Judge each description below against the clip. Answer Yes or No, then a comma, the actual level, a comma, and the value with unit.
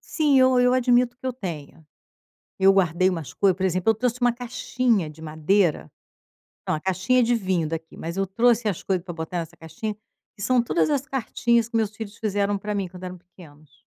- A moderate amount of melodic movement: No, wide, 5.7 semitones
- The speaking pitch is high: Yes, high, 200 Hz